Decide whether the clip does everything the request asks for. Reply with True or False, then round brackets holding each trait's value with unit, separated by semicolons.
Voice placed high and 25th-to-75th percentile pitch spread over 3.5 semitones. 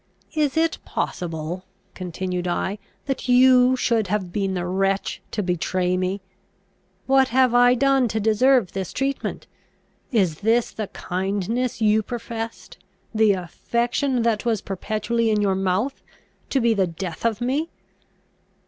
True (215 Hz; 4.8 semitones)